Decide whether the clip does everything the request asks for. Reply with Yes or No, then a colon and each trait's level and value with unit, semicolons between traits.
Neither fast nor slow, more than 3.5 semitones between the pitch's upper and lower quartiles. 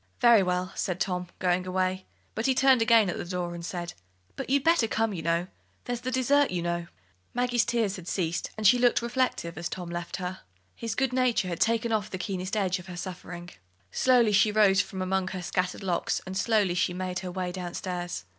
No: fast, 215 wpm; average, 4.4 semitones